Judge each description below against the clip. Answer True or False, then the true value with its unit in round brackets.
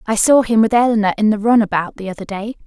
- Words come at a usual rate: False (270 wpm)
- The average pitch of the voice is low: False (220 Hz)